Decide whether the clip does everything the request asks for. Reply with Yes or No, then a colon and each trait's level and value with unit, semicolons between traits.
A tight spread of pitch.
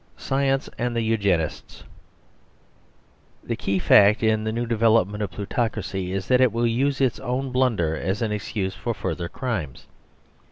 No: average, 3.9 semitones